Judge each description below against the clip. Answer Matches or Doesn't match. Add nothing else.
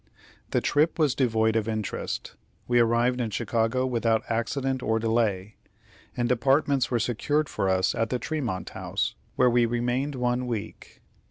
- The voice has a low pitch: Matches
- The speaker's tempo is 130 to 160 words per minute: Matches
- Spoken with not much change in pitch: Matches